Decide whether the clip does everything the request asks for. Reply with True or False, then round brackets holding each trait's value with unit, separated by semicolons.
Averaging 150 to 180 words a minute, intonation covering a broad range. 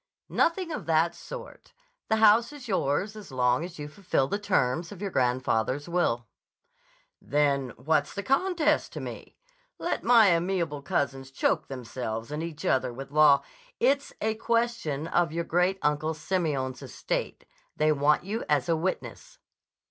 True (155 wpm; 6.4 semitones)